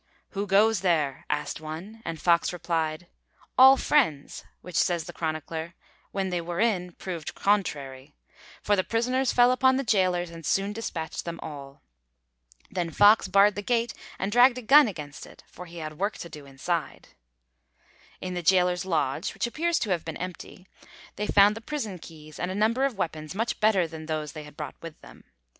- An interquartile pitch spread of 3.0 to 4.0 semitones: No, average, 4.9 semitones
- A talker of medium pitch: Yes, medium, 180 Hz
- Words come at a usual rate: Yes, average, 185 wpm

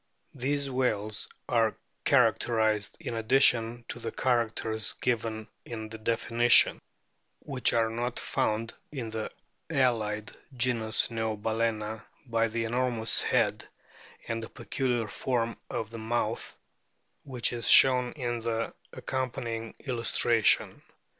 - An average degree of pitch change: No, narrow, 1.7 semitones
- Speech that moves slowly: Yes, slow, 115 wpm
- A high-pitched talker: No, low, 115 Hz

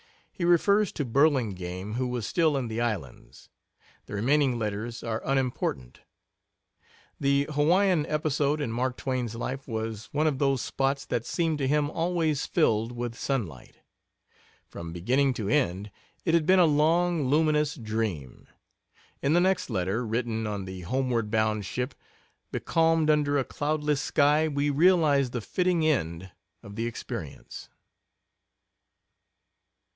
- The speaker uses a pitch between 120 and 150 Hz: Yes, low, 135 Hz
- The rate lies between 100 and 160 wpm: Yes, average, 140 wpm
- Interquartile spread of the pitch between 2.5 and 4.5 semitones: No, wide, 5.4 semitones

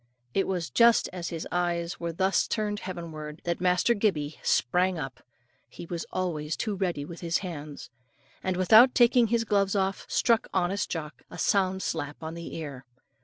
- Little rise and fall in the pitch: No, average, 3.3 semitones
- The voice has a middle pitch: Yes, medium, 180 Hz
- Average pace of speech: Yes, average, 170 wpm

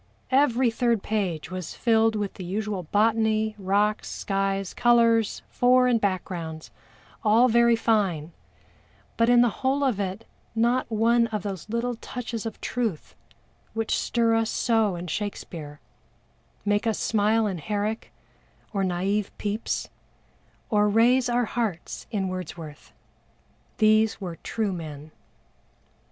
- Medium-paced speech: No, slow, 130 wpm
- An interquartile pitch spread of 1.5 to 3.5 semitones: Yes, average, 3.2 semitones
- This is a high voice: Yes, high, 215 Hz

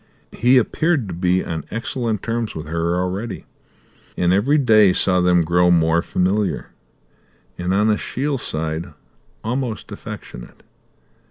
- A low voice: Yes, very low, 95 Hz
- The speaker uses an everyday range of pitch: Yes, average, 4.9 semitones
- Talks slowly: Yes, slow, 125 wpm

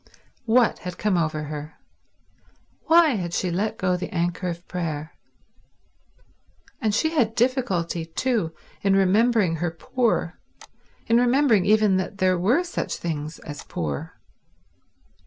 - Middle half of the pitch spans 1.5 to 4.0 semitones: No, wide, 5.5 semitones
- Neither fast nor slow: No, slow, 130 wpm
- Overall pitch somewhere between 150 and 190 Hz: Yes, medium, 185 Hz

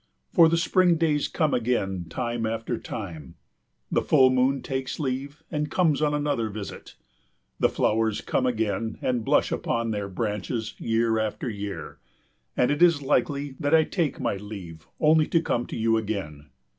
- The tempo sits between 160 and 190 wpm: Yes, average, 165 wpm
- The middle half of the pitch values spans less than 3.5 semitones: No, average, 5.3 semitones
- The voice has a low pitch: Yes, low, 120 Hz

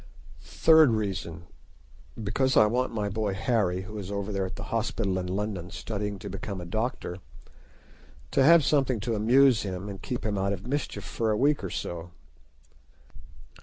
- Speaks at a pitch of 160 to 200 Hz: No, low, 105 Hz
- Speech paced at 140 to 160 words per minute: No, average, 170 wpm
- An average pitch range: Yes, average, 4.0 semitones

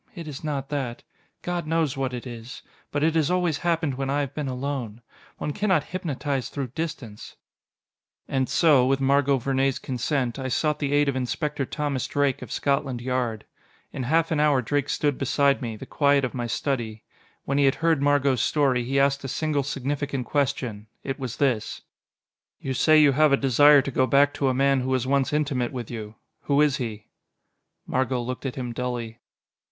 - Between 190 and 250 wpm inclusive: Yes, average, 195 wpm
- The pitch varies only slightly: Yes, narrow, 2.3 semitones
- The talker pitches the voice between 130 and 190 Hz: Yes, low, 135 Hz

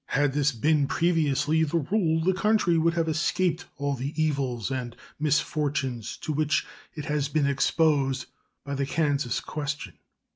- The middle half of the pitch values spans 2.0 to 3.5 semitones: Yes, average, 2.7 semitones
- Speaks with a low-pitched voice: No, medium, 150 Hz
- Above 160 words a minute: No, average, 150 wpm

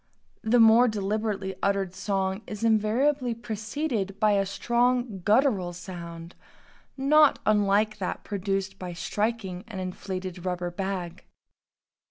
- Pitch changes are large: No, average, 3.2 semitones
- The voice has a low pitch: No, high, 200 Hz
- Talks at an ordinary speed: No, slow, 115 wpm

